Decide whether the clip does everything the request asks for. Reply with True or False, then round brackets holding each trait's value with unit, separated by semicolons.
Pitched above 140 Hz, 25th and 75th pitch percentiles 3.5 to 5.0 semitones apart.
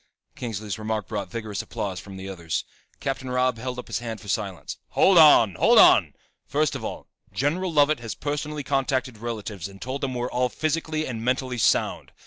False (125 Hz; 4.6 semitones)